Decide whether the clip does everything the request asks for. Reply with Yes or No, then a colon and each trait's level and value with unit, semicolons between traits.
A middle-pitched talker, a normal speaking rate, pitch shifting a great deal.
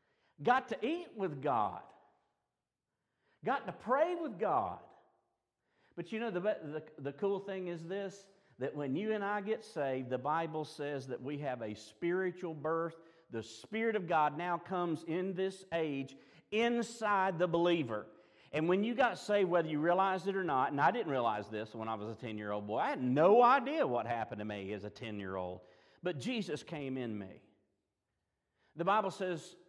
Yes: medium, 165 Hz; average, 190 wpm; wide, 7.9 semitones